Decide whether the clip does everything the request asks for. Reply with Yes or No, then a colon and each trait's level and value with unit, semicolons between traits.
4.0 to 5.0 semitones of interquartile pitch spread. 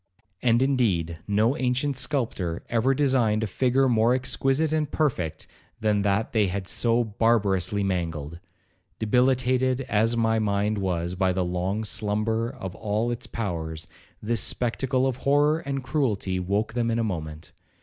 Yes: average, 4.7 semitones